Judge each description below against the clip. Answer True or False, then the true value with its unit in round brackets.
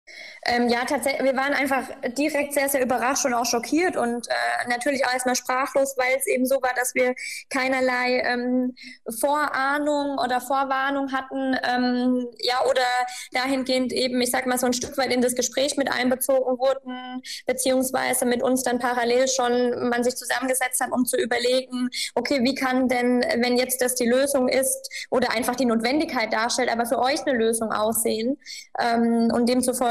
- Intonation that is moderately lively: False (1.4 semitones)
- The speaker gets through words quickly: False (175 wpm)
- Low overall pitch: False (255 Hz)